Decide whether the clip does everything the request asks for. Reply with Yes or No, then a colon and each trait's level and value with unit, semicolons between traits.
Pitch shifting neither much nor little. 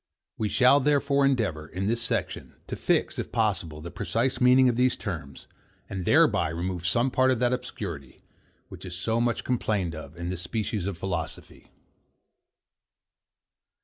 No: wide, 6.5 semitones